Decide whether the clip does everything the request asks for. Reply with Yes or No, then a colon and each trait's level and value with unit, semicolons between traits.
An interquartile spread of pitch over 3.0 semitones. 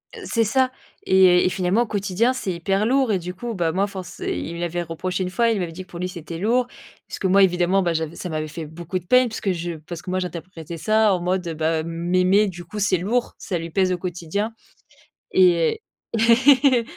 Yes: average, 3.6 semitones